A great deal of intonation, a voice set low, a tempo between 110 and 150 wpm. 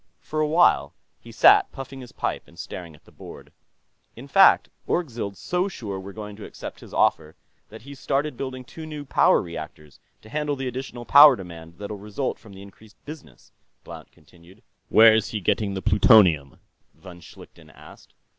No: wide, 6.4 semitones; low, 110 Hz; average, 180 wpm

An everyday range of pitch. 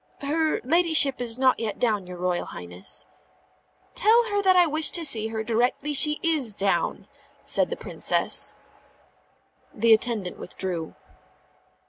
No: wide, 7.3 semitones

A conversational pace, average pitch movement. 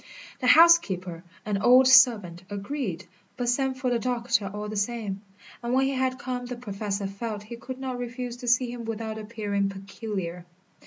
Yes: average, 175 wpm; average, 3.8 semitones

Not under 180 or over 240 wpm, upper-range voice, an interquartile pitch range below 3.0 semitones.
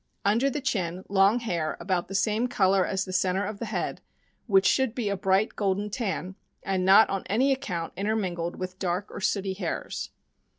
Yes: average, 185 wpm; high, 195 Hz; narrow, 2.6 semitones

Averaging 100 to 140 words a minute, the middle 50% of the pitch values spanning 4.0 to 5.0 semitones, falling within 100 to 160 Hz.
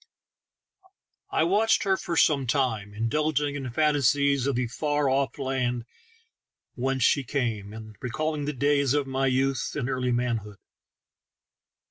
No: slow, 135 wpm; average, 3.1 semitones; low, 135 Hz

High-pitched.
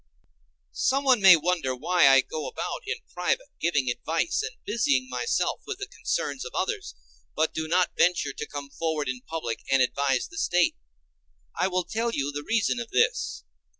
No: medium, 160 Hz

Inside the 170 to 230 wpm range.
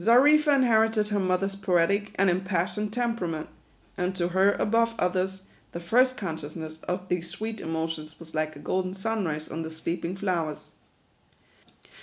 No: average, 150 wpm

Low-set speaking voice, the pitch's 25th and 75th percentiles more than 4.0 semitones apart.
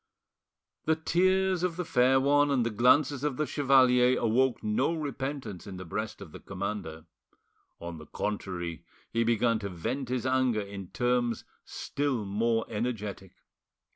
Yes: low, 120 Hz; average, 5.0 semitones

